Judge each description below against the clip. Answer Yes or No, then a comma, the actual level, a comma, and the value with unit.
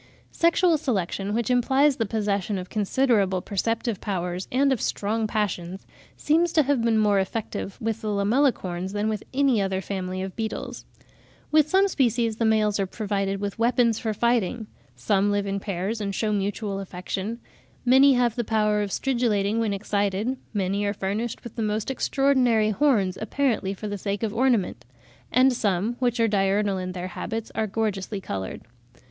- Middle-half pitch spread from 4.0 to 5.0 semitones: No, average, 3.3 semitones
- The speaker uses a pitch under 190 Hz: No, high, 215 Hz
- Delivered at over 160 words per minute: Yes, average, 170 wpm